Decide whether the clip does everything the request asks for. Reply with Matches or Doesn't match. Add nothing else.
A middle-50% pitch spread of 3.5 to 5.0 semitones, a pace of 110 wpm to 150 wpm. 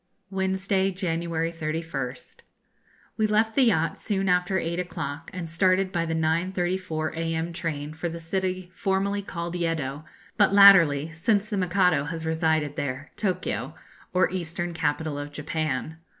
Doesn't match